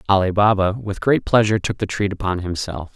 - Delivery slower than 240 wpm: Yes, fast, 205 wpm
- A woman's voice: No, male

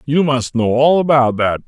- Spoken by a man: Yes, male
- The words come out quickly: Yes, fast, 215 wpm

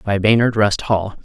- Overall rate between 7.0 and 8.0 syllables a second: No, 4.5 syllables/s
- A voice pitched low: Yes, low, 105 Hz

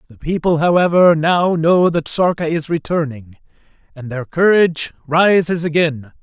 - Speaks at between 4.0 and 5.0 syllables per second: Yes, 4.6 syllables/s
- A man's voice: Yes, male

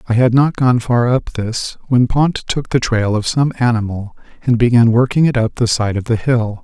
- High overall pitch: No, low, 120 Hz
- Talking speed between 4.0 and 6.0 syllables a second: Yes, 4.8 syllables/s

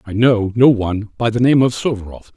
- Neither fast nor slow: No, fast, 230 wpm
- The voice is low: Yes, low, 115 Hz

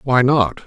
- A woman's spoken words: No, male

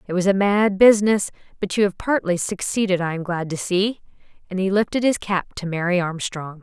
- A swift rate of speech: Yes, fast, 210 wpm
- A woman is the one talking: Yes, female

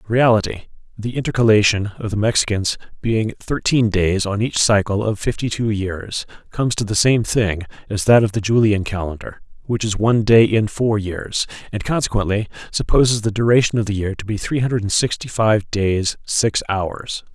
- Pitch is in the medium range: No, low, 105 Hz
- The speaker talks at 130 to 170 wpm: No, average, 185 wpm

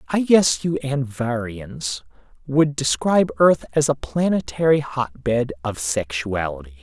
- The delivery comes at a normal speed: No, slow, 115 wpm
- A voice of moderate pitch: No, low, 125 Hz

